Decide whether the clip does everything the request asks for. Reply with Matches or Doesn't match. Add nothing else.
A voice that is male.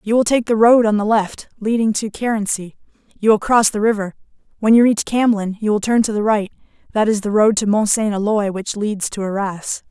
Doesn't match